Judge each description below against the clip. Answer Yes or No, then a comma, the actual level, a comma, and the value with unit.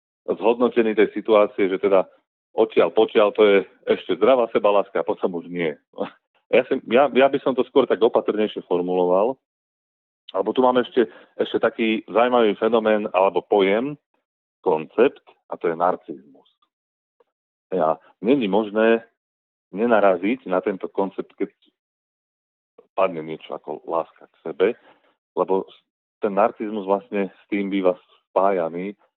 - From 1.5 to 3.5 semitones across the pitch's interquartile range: No, average, 4.4 semitones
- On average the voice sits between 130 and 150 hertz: No, low, 105 Hz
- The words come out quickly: No, average, 135 wpm